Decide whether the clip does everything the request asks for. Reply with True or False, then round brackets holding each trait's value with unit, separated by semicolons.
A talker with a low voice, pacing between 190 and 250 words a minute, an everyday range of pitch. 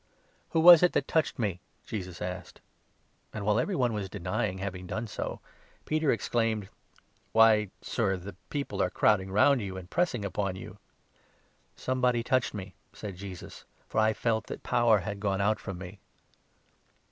True (105 Hz; 195 wpm; 3.9 semitones)